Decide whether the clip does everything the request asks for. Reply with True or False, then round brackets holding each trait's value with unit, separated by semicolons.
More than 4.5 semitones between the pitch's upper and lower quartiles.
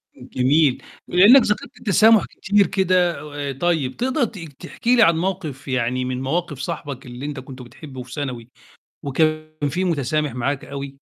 True (5.5 semitones)